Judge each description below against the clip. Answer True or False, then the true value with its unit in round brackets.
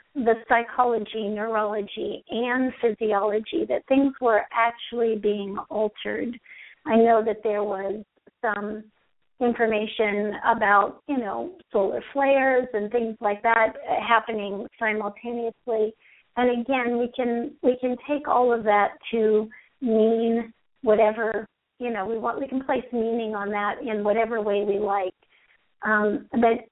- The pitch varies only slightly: True (2.2 semitones)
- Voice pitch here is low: False (225 Hz)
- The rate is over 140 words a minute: False (135 wpm)